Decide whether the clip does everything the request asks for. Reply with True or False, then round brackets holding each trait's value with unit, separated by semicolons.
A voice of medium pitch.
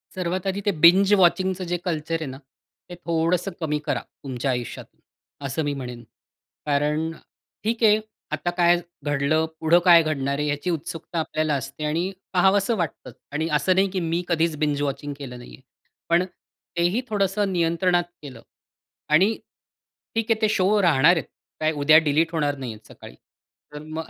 True (165 Hz)